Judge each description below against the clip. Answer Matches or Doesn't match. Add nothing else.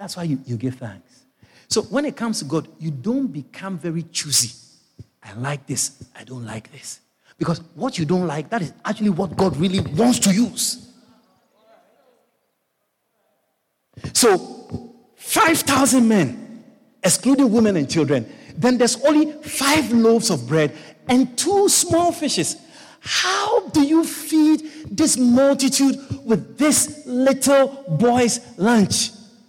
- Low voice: Doesn't match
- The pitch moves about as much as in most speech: Doesn't match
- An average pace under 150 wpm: Matches